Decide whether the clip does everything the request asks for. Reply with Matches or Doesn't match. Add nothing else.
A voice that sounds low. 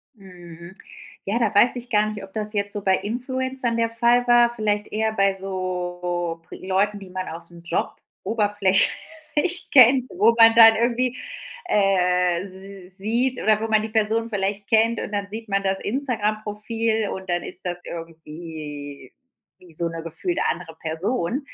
Doesn't match